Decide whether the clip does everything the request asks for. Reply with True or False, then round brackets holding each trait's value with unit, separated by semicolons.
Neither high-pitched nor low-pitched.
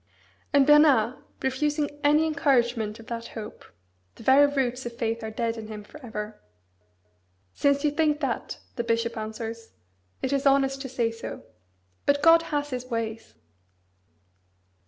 False (255 Hz)